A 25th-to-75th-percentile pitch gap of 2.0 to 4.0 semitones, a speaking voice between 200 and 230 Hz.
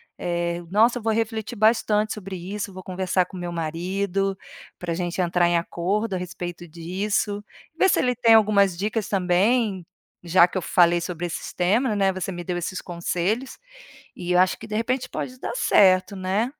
No: average, 3.4 semitones; high, 190 Hz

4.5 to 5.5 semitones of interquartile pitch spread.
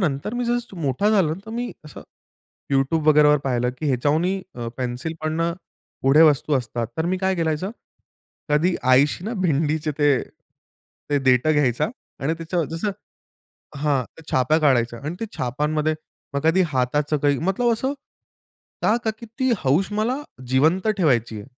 Yes: average, 5.1 semitones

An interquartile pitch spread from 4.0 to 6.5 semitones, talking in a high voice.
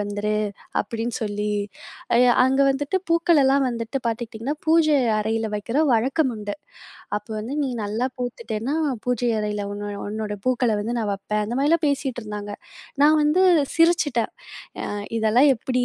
Yes: average, 4.6 semitones; high, 235 Hz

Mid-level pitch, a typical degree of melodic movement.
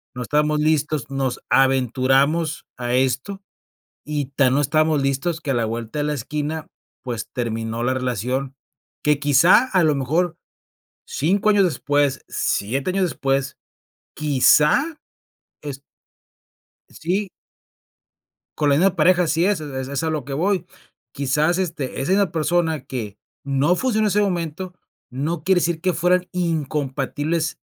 Yes: medium, 150 Hz; average, 4.3 semitones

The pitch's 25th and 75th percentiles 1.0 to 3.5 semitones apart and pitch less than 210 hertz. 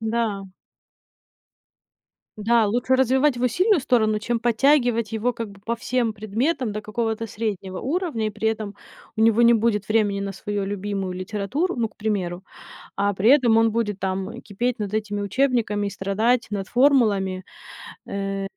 No: average, 3.0 semitones; high, 220 Hz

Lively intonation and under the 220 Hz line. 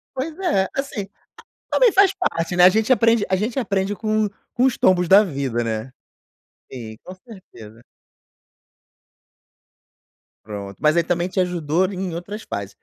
Yes: wide, 6.3 semitones; medium, 185 Hz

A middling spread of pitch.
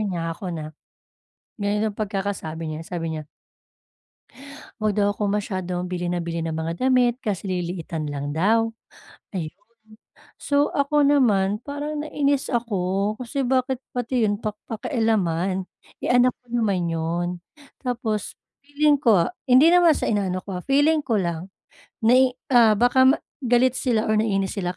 No: wide, 5.9 semitones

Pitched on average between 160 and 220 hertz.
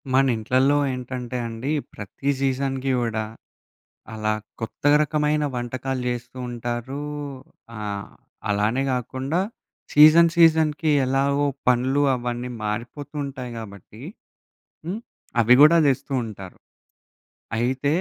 No: low, 130 Hz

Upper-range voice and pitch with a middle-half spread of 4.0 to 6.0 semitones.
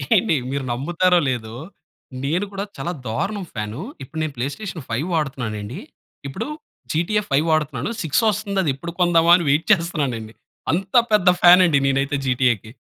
No: medium, 155 Hz; wide, 5.5 semitones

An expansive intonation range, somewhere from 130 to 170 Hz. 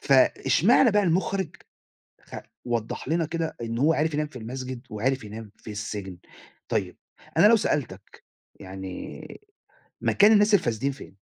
Yes: wide, 7.1 semitones; low, 135 Hz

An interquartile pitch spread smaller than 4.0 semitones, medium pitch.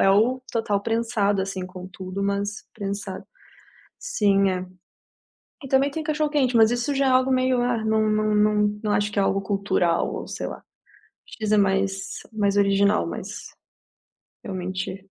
No: average, 3.0 semitones; high, 205 Hz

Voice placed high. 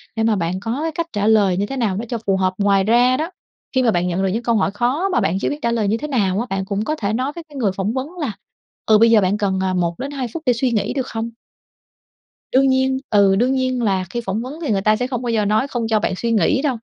Yes: high, 225 Hz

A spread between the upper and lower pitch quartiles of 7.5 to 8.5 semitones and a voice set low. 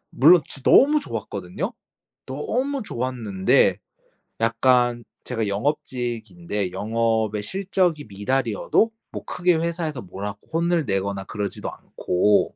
Yes: wide, 7.8 semitones; low, 120 Hz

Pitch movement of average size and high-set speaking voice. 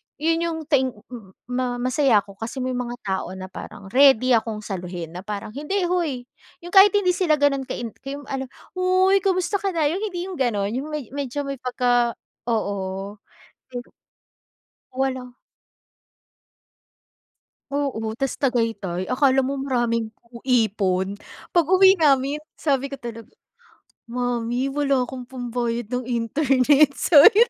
Yes: average, 4.1 semitones; very high, 255 Hz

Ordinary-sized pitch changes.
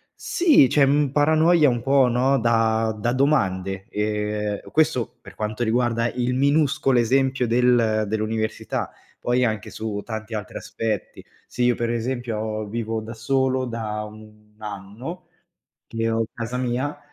Yes: average, 3.1 semitones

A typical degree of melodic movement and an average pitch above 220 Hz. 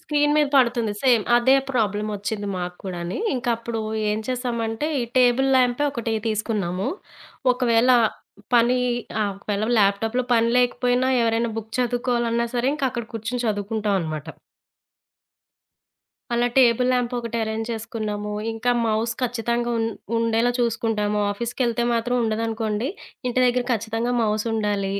No: narrow, 2.3 semitones; high, 230 Hz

